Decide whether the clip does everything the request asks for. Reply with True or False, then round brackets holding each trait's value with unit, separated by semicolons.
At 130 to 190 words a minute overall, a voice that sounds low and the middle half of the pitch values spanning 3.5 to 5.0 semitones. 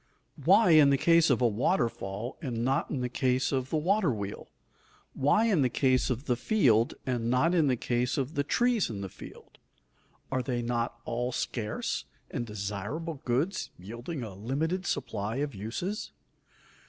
True (170 wpm; 125 Hz; 4.6 semitones)